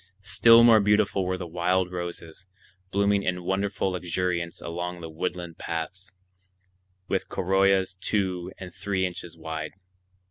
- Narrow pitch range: Yes, narrow, 2.0 semitones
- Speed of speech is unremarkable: No, slow, 130 wpm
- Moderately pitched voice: No, very low, 90 Hz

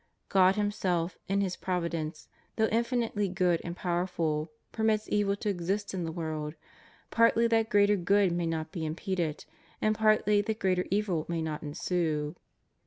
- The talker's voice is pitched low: No, medium, 185 Hz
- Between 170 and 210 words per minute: No, average, 155 wpm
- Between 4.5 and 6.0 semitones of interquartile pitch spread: No, average, 3.7 semitones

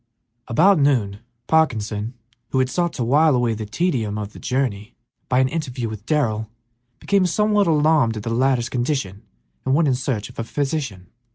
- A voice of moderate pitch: No, low, 130 Hz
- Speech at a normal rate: Yes, average, 175 wpm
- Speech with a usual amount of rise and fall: No, wide, 5.7 semitones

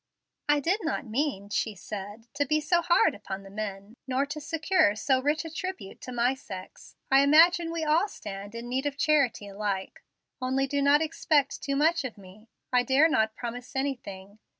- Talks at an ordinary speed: Yes, average, 190 wpm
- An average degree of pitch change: No, wide, 6.2 semitones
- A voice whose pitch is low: No, very high, 265 Hz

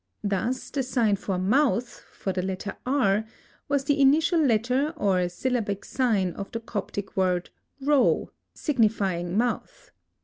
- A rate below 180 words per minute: Yes, slow, 135 wpm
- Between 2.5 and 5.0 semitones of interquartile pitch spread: No, wide, 5.6 semitones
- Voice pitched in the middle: No, high, 225 Hz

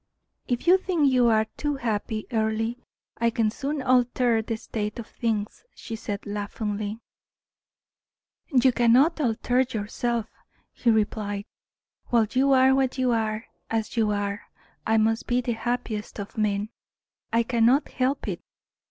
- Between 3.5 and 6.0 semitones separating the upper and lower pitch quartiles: No, average, 2.8 semitones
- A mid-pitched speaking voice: No, high, 230 Hz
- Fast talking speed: No, average, 145 wpm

